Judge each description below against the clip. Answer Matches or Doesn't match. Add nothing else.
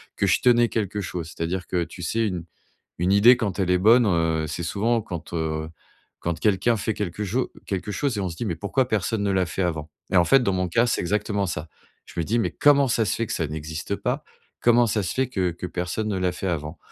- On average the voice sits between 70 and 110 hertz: Matches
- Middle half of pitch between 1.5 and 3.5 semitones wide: Doesn't match